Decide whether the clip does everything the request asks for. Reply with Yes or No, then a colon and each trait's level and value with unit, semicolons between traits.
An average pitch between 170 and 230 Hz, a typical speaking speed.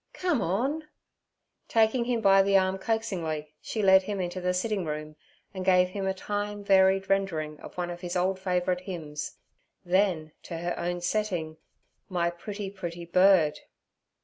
Yes: medium, 185 Hz; average, 155 wpm